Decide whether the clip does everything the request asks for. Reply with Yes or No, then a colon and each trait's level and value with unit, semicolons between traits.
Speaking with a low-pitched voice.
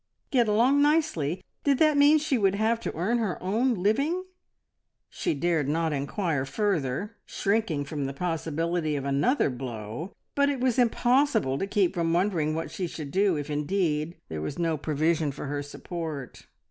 No: medium, 175 Hz